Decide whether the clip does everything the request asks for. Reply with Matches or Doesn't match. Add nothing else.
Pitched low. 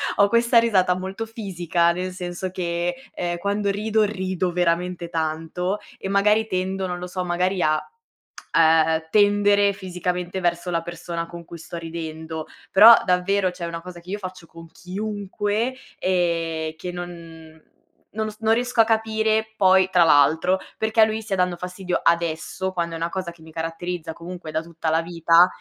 Doesn't match